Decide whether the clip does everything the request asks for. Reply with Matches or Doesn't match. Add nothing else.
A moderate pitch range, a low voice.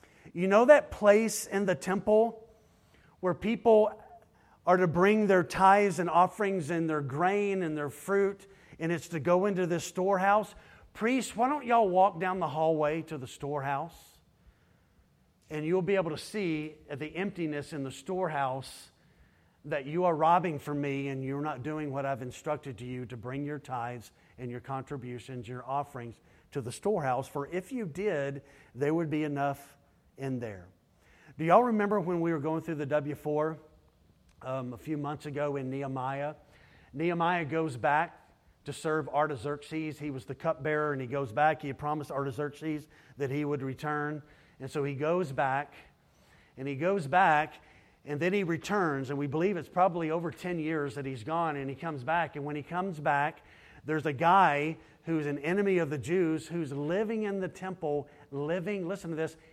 Doesn't match